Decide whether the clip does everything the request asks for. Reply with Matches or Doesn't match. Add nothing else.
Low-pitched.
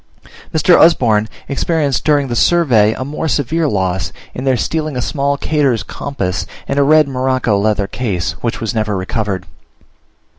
Matches